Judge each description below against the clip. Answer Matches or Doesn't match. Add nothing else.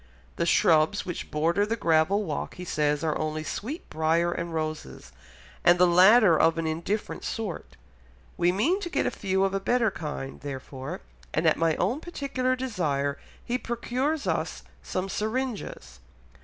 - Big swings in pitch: Matches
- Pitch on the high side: Doesn't match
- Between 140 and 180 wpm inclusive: Matches